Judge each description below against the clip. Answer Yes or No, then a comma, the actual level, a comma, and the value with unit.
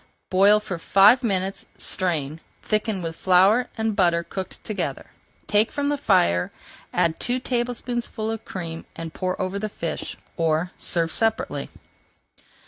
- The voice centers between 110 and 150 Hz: No, high, 195 Hz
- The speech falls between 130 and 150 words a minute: Yes, slow, 135 wpm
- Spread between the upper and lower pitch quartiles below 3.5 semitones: No, average, 4.7 semitones